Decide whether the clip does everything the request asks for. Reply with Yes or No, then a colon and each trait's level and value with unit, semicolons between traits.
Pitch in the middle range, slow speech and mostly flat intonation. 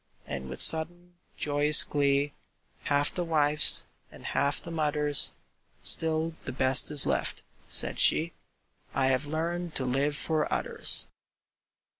Yes: medium, 150 Hz; slow, 130 wpm; narrow, 2.3 semitones